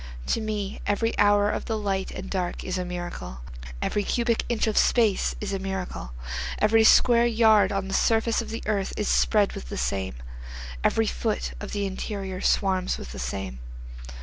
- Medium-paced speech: Yes, average, 180 wpm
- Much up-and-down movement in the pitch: No, average, 3.0 semitones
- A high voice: Yes, high, 195 Hz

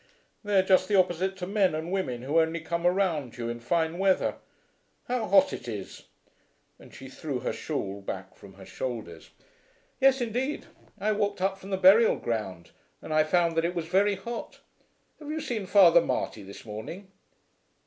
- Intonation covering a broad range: Yes, wide, 7.7 semitones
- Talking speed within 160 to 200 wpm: Yes, average, 180 wpm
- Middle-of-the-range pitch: Yes, medium, 175 Hz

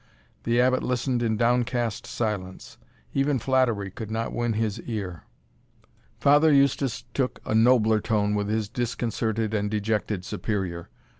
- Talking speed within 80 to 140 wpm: Yes, slow, 135 wpm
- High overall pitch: No, low, 115 Hz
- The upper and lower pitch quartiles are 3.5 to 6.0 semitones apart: No, average, 2.9 semitones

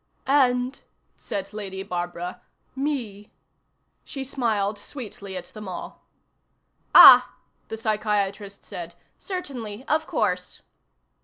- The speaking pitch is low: No, high, 210 Hz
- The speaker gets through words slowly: Yes, slow, 95 wpm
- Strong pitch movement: No, average, 4.5 semitones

